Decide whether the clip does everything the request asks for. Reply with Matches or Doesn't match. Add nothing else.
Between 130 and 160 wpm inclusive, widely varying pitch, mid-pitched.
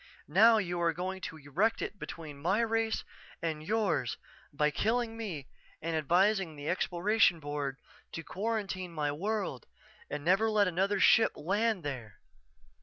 Matches